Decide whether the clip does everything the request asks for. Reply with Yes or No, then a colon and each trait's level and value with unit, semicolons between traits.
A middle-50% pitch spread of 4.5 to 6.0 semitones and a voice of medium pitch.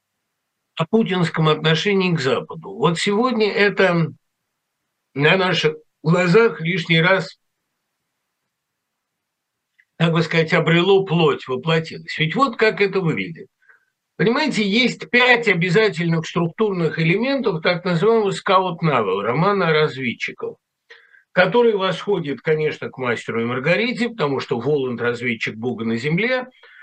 Yes: average, 5.3 semitones; medium, 180 Hz